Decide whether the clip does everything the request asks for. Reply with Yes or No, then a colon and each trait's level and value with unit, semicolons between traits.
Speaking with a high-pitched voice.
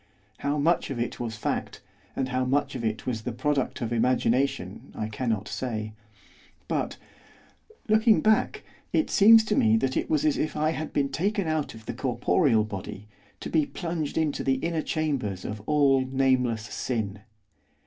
No: low, 130 Hz